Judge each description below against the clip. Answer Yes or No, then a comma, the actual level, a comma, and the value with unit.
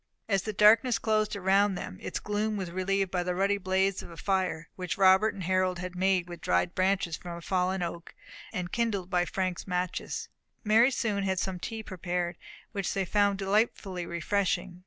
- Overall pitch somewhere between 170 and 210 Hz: Yes, high, 190 Hz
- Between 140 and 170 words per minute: No, average, 185 wpm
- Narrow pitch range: Yes, narrow, 2.1 semitones